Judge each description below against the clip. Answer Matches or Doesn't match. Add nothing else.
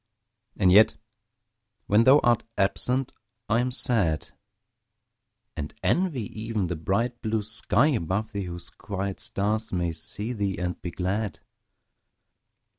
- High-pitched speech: Doesn't match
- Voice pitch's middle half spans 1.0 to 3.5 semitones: Doesn't match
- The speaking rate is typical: Doesn't match